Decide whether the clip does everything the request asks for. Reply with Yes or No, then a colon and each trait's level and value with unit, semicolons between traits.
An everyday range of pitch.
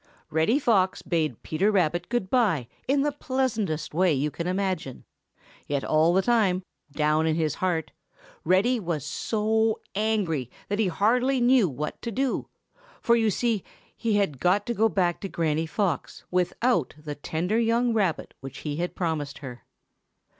No: wide, 5.9 semitones